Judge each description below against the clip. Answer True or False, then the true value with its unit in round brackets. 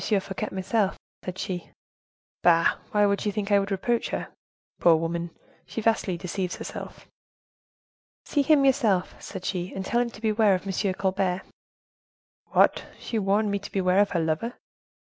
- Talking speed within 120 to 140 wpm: False (160 wpm)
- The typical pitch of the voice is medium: False (195 Hz)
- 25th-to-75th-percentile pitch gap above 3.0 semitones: False (2.7 semitones)